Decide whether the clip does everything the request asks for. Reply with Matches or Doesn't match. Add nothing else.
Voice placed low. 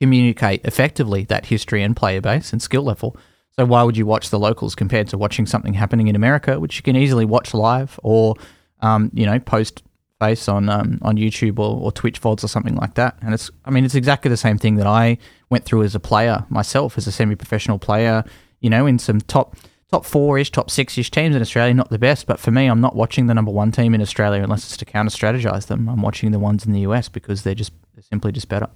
Matches